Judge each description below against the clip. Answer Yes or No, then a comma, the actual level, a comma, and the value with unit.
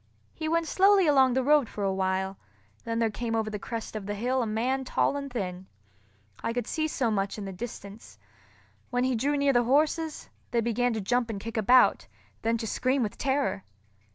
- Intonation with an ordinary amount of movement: Yes, average, 3.9 semitones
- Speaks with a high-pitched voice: Yes, high, 235 Hz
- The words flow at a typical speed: No, fast, 210 wpm